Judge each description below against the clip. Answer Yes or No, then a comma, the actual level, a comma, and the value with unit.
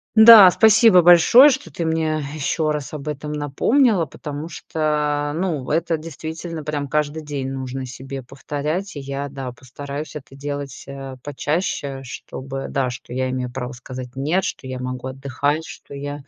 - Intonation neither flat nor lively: Yes, average, 3.1 semitones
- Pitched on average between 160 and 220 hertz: No, medium, 145 Hz